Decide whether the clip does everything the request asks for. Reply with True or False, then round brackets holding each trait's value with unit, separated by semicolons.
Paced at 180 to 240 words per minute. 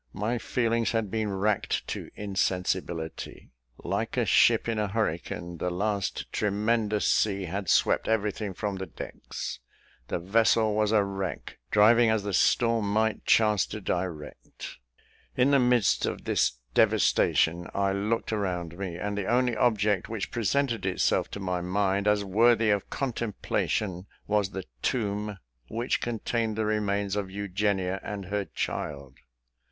False (145 wpm)